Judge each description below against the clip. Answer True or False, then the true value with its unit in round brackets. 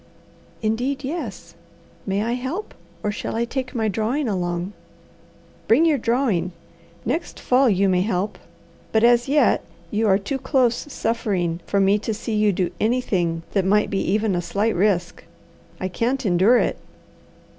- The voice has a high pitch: True (215 Hz)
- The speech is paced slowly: False (155 wpm)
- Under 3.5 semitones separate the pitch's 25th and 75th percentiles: False (4.5 semitones)